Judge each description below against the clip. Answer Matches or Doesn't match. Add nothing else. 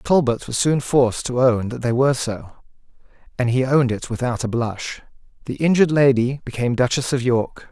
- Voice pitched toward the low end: Matches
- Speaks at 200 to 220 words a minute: Doesn't match